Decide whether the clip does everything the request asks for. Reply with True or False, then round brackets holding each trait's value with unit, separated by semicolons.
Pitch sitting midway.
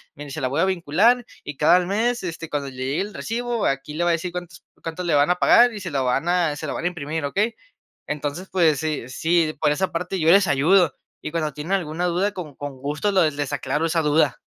True (165 Hz)